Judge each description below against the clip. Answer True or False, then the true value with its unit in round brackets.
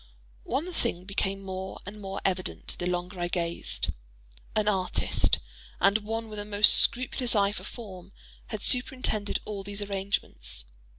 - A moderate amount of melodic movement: False (2.3 semitones)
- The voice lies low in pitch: False (200 Hz)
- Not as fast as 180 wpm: True (145 wpm)